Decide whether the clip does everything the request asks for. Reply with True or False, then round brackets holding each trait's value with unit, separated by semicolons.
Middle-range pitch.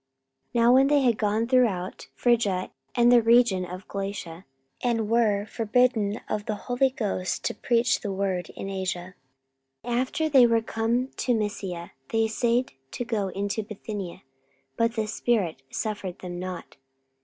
False (220 Hz)